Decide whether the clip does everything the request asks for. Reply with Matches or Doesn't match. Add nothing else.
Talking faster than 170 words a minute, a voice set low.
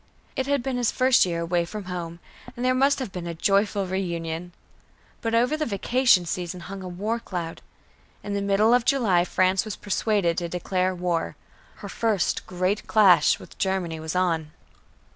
Doesn't match